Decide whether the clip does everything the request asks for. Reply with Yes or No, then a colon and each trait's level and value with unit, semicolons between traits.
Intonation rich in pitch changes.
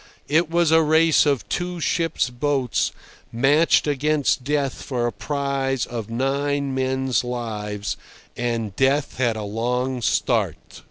No: average, 3.5 semitones